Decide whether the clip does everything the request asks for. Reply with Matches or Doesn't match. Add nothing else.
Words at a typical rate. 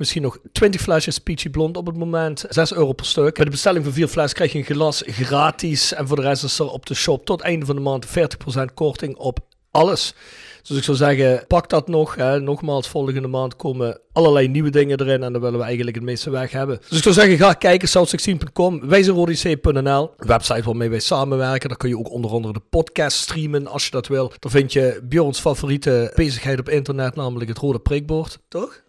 Doesn't match